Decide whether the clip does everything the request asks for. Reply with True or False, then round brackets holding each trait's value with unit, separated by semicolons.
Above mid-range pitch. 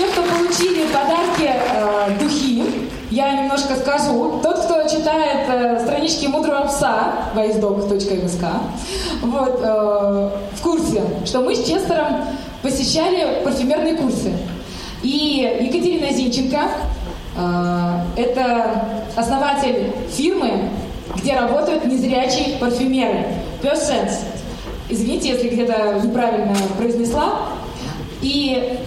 True (260 Hz)